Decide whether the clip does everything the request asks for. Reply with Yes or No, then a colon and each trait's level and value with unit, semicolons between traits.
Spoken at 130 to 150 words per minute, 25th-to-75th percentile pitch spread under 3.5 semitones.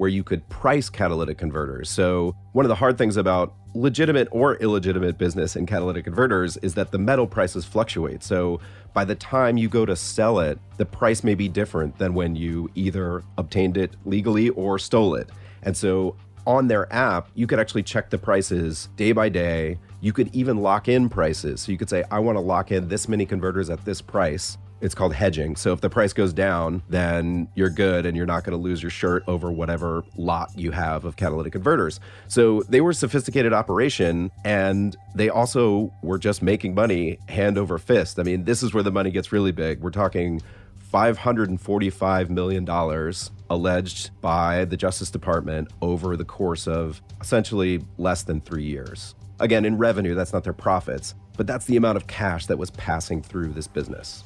No: average, 195 wpm; average, 2.9 semitones